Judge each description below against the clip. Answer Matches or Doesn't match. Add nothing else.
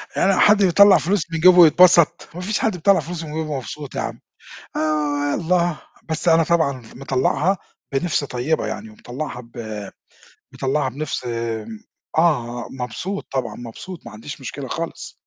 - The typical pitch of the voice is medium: Matches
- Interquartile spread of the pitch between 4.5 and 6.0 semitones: Matches